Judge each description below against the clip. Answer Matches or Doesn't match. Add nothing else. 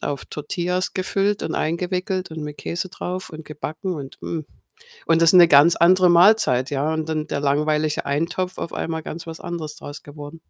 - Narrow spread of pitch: Doesn't match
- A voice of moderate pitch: Matches